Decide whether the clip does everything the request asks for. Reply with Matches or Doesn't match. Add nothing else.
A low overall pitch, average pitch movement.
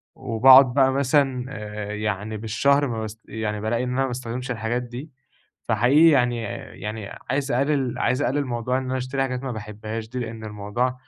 Matches